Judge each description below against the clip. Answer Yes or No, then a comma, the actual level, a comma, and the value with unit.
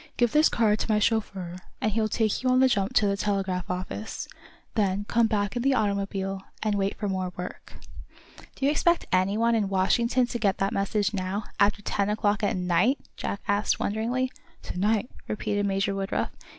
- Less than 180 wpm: No, average, 190 wpm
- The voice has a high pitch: Yes, high, 205 Hz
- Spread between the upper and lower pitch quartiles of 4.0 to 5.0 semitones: No, narrow, 2.4 semitones